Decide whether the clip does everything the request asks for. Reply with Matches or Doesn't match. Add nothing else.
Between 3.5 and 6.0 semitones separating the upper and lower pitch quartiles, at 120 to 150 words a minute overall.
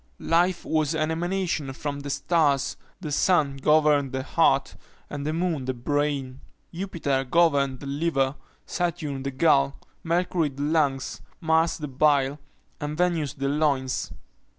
Doesn't match